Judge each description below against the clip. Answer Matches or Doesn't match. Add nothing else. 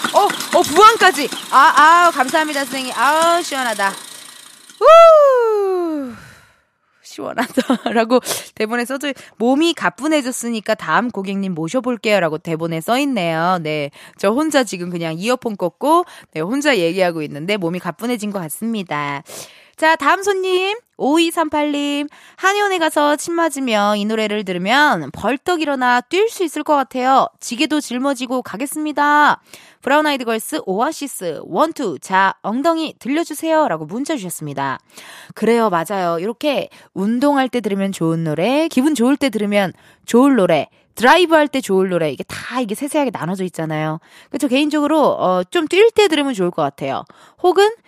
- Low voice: Doesn't match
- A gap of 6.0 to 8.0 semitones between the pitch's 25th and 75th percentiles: Matches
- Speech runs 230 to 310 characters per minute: Doesn't match